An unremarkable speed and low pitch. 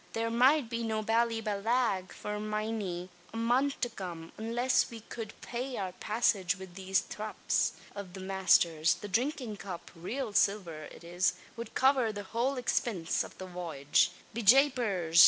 No: average, 155 wpm; high, 215 Hz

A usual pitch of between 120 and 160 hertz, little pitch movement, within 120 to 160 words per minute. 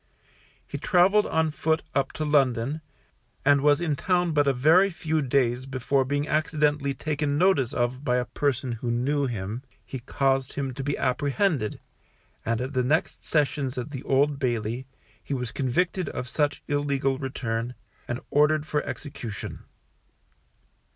No: medium, 140 Hz; average, 3.0 semitones; average, 155 wpm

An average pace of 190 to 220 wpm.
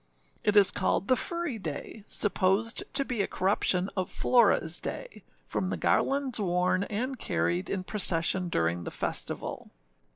No: average, 150 wpm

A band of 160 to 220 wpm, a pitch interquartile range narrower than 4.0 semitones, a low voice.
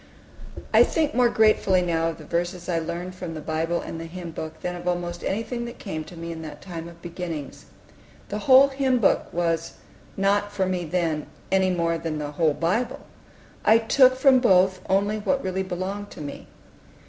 No: average, 195 wpm; average, 3.6 semitones; medium, 180 Hz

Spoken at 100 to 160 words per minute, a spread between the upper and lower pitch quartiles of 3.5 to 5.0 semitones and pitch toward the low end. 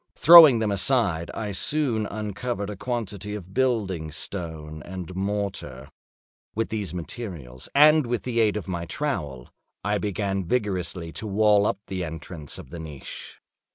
Yes: average, 150 wpm; average, 4.7 semitones; low, 100 Hz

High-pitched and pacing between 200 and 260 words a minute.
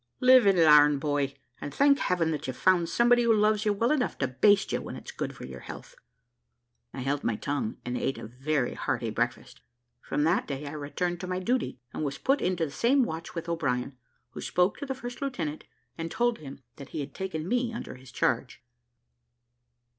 No: medium, 165 Hz; fast, 205 wpm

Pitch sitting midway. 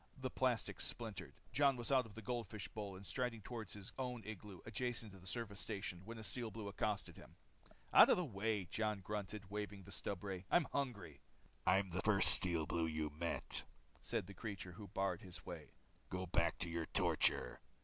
No: low, 100 Hz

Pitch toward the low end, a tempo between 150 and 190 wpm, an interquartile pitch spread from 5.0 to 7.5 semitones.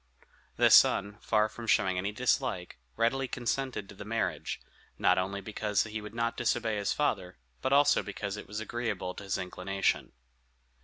No: low, 105 Hz; average, 165 wpm; average, 3.0 semitones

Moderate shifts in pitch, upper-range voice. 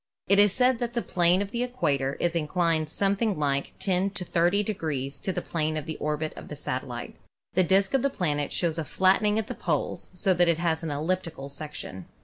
No: average, 4.4 semitones; medium, 175 Hz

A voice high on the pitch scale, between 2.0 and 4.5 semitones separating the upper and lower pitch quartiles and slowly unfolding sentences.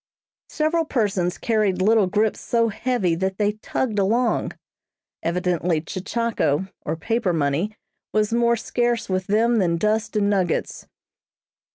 Yes: high, 210 Hz; average, 4.2 semitones; slow, 130 wpm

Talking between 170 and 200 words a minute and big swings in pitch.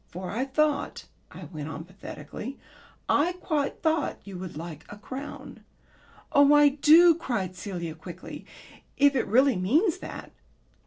No: average, 145 wpm; wide, 8.3 semitones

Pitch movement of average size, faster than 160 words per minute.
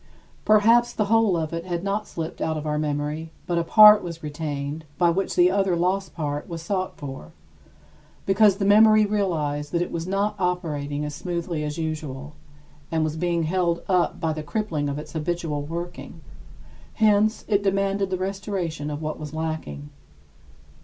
Yes: average, 4.3 semitones; average, 175 wpm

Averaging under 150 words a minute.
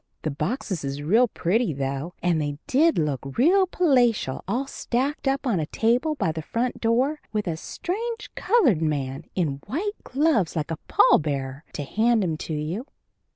No: average, 175 wpm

